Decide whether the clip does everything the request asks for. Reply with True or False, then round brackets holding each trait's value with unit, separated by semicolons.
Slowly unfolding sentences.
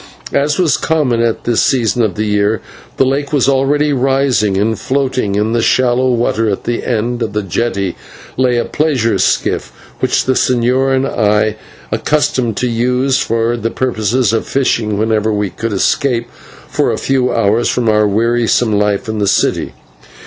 False (175 wpm)